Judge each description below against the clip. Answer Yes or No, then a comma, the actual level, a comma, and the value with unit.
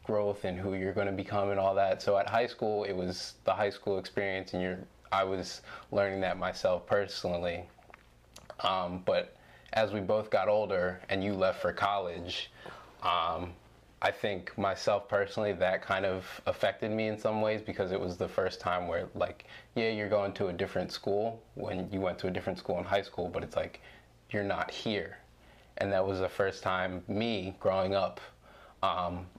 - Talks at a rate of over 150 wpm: Yes, average, 190 wpm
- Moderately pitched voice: No, low, 100 Hz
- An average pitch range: No, narrow, 2.0 semitones